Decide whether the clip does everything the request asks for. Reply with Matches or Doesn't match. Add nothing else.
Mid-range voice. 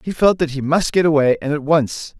Matches